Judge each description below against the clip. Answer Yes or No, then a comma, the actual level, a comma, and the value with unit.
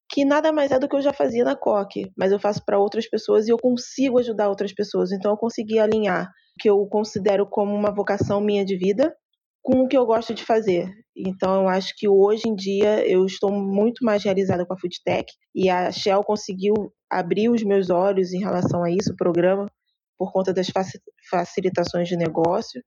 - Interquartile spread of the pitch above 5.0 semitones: No, average, 3.1 semitones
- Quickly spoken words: Yes, fast, 205 wpm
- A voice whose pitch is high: Yes, high, 205 Hz